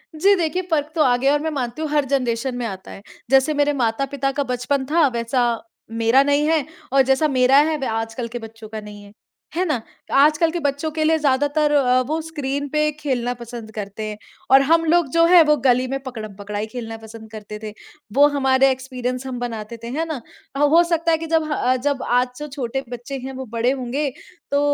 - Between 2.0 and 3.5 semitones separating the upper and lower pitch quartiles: No, average, 3.9 semitones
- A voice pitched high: Yes, very high, 270 Hz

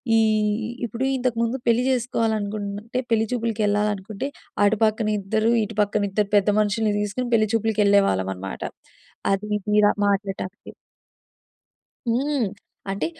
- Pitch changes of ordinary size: No, narrow, 2.0 semitones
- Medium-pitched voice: No, high, 215 Hz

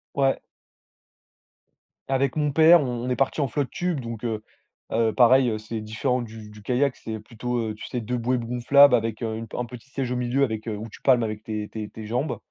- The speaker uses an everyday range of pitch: Yes, average, 3.1 semitones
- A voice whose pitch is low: Yes, low, 120 Hz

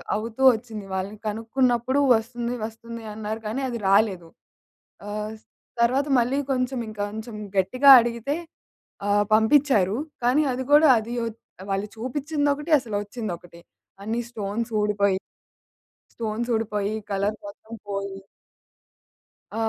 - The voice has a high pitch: Yes, high, 220 Hz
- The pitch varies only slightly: No, average, 3.1 semitones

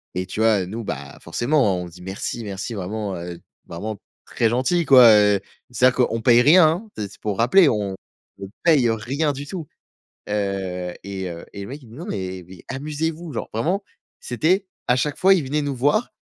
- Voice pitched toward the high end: No, low, 115 Hz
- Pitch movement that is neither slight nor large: No, wide, 7.0 semitones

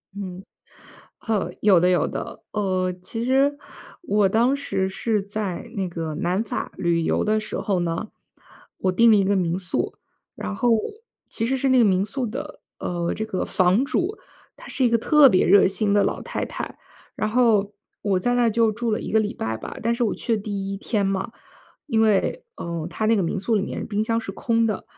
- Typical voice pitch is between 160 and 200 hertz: No, high, 210 Hz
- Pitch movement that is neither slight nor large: Yes, average, 3.6 semitones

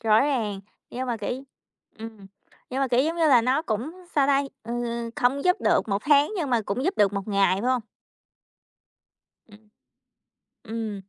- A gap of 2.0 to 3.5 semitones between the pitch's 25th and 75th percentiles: No, average, 4.5 semitones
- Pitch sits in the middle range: No, high, 240 Hz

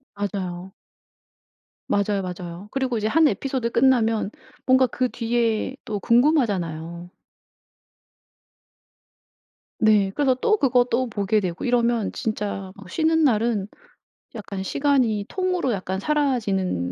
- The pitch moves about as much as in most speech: Yes, average, 5.0 semitones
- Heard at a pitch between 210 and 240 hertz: Yes, high, 220 Hz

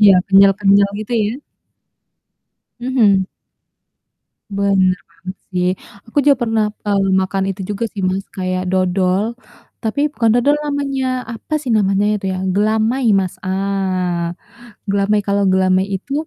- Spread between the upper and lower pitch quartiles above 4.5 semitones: No, average, 3.0 semitones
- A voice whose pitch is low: No, high, 200 Hz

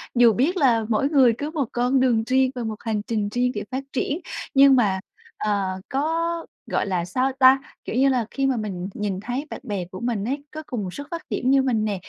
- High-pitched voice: Yes, very high, 250 Hz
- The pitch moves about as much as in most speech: Yes, average, 4.3 semitones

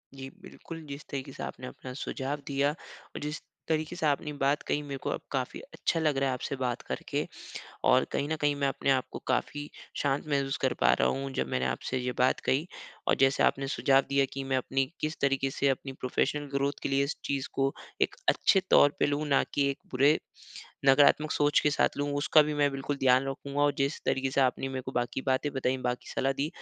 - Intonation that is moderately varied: No, narrow, 1.5 semitones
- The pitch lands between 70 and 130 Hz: No, medium, 140 Hz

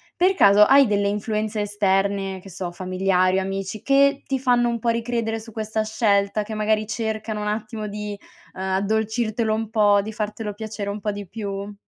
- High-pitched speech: Yes, high, 210 Hz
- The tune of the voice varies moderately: No, narrow, 1.7 semitones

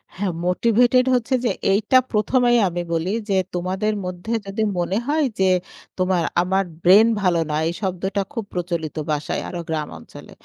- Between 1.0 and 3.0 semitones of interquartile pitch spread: No, average, 3.9 semitones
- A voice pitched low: No, high, 190 Hz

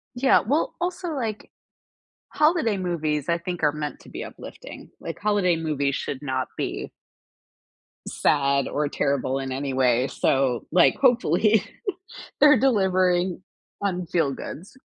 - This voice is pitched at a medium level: Yes, medium, 170 Hz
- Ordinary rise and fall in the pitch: No, wide, 7.2 semitones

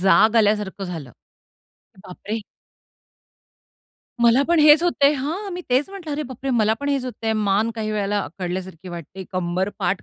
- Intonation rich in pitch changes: Yes, wide, 6.5 semitones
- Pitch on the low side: No, high, 215 Hz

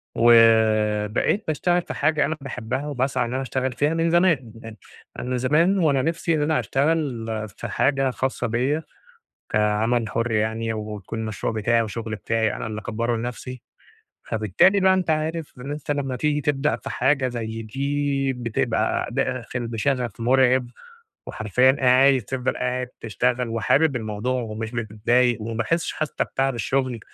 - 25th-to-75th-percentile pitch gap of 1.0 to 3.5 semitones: No, average, 4.0 semitones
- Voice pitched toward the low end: Yes, low, 125 Hz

